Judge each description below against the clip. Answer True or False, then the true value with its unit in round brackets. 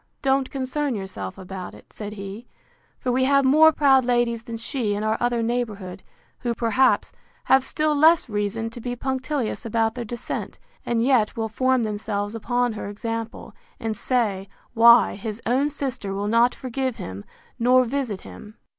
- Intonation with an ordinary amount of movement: True (3.4 semitones)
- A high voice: True (235 Hz)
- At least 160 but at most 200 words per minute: True (165 wpm)